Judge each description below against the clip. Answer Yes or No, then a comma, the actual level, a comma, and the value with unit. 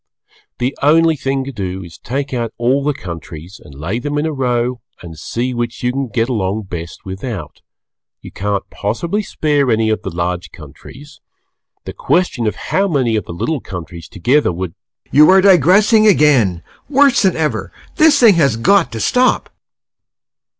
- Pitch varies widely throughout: Yes, wide, 8.0 semitones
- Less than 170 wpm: No, average, 175 wpm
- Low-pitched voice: Yes, low, 125 Hz